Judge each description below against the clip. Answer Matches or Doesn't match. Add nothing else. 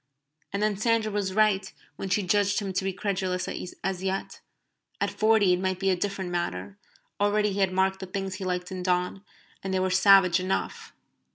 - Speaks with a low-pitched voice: Doesn't match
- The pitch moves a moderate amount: Doesn't match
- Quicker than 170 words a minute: Matches